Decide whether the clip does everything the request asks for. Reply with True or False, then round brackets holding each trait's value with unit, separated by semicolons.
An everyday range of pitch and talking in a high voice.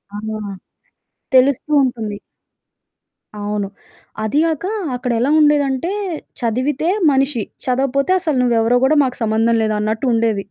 True (3.6 semitones; 250 Hz)